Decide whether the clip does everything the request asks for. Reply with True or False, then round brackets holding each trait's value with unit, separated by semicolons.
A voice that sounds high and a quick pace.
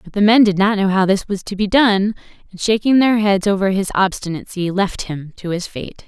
True (195 Hz; 235 wpm)